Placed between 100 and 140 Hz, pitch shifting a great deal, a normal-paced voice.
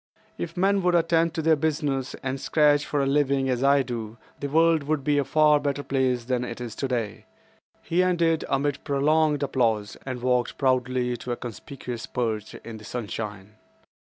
No: low, 135 Hz; average, 3.6 semitones; average, 180 wpm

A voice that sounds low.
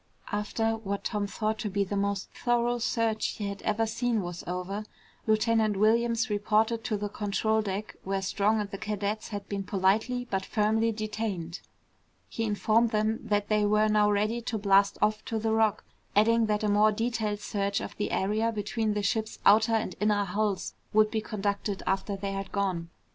No: high, 210 Hz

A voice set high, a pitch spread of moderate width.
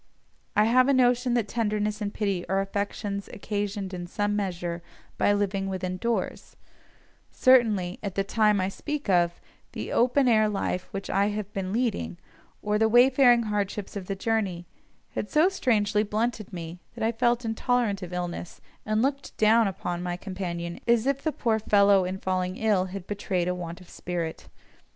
Yes: high, 205 Hz; average, 3.5 semitones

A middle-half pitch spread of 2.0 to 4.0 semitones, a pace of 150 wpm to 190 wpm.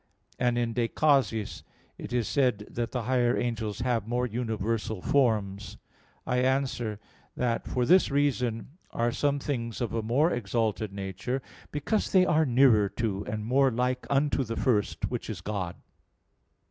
Yes: average, 3.2 semitones; average, 155 wpm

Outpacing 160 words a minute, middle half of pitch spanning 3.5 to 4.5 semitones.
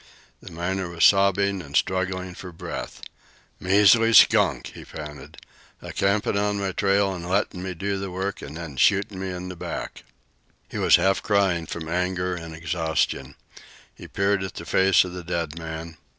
No: average, 175 wpm; average, 2.7 semitones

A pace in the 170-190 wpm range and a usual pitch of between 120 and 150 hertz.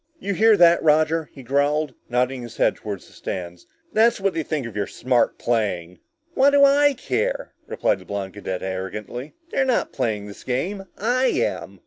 Yes: average, 180 wpm; medium, 140 Hz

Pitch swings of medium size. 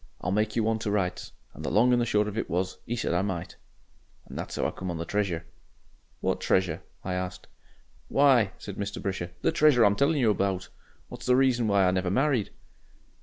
Yes: average, 4.2 semitones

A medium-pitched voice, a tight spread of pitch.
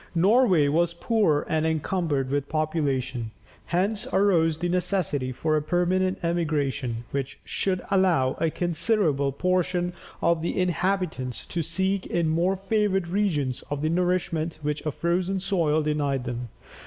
No: medium, 170 Hz; average, 3.8 semitones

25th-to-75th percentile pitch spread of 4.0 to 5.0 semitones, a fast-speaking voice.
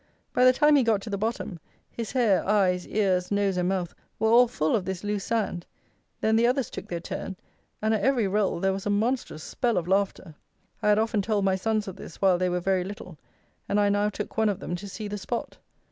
No: average, 2.8 semitones; fast, 240 wpm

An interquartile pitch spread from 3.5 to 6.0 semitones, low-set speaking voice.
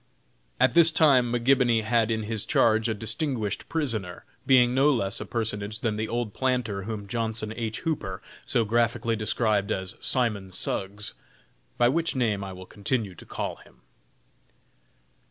No: average, 2.9 semitones; low, 110 Hz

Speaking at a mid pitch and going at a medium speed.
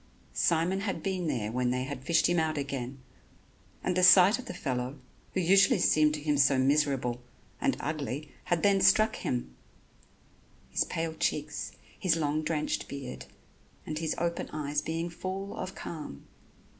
Yes: medium, 155 Hz; average, 160 wpm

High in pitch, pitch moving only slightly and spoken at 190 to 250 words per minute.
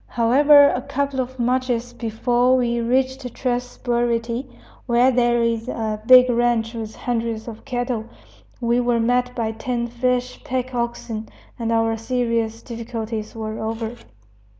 No: high, 240 Hz; narrow, 1.6 semitones; average, 140 wpm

